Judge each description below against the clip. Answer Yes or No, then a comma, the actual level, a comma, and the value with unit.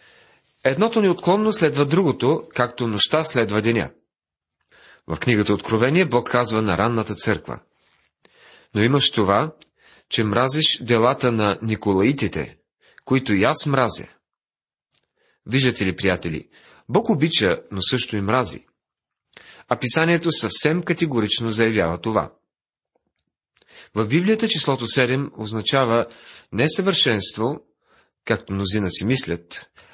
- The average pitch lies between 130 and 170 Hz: No, low, 120 Hz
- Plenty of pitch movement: Yes, wide, 6.3 semitones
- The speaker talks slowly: Yes, slow, 105 wpm